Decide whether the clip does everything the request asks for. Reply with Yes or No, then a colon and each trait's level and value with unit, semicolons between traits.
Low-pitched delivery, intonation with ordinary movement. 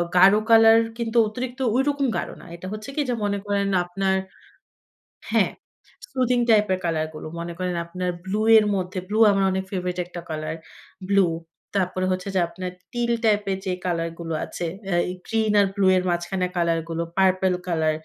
No: high, 190 Hz; average, 3.2 semitones